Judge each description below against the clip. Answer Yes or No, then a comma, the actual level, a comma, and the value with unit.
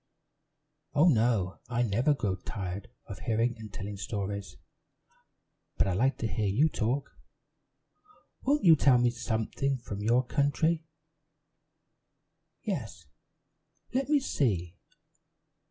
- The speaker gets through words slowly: Yes, slow, 115 wpm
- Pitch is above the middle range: No, low, 115 Hz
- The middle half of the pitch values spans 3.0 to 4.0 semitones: No, wide, 5.6 semitones